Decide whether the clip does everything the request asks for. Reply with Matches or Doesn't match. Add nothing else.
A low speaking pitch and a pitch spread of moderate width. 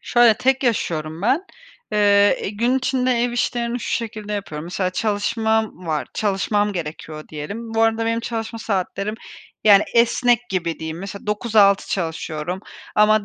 Doesn't match